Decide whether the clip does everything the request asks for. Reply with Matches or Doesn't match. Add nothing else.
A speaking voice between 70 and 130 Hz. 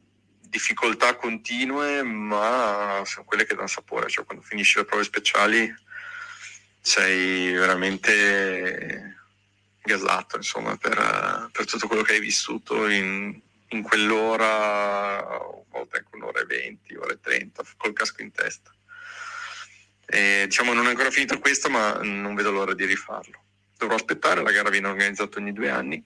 Matches